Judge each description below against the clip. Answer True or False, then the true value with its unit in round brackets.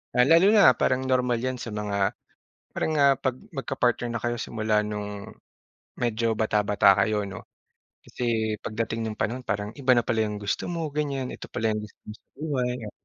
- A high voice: False (115 Hz)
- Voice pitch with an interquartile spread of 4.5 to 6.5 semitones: False (3.5 semitones)